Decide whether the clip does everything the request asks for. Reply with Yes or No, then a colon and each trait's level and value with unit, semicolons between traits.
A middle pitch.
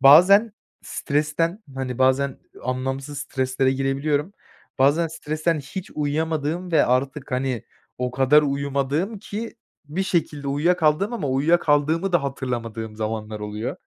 Yes: medium, 145 Hz